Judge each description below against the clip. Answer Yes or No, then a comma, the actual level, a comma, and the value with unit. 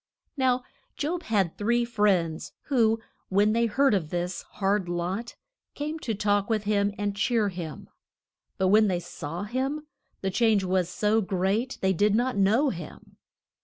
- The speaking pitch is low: No, high, 205 Hz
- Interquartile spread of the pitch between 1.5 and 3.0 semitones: No, average, 3.8 semitones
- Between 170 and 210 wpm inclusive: No, average, 160 wpm